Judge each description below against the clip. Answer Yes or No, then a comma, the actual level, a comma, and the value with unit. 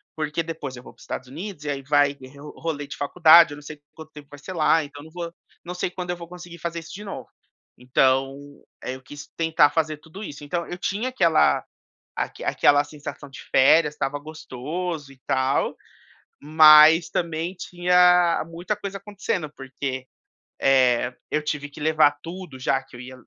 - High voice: No, medium, 155 Hz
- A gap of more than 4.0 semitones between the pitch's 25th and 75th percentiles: No, average, 3.2 semitones